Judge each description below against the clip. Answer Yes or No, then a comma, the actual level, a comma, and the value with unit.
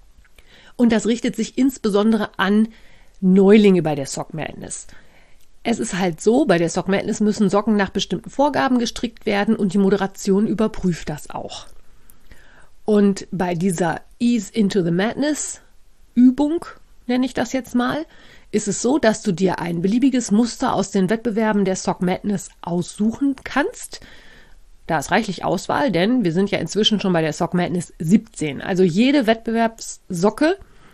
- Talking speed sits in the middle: Yes, average, 155 wpm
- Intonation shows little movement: No, average, 3.7 semitones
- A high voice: Yes, high, 210 Hz